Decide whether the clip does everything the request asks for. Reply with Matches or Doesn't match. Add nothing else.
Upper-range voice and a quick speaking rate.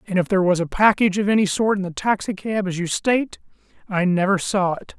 Matches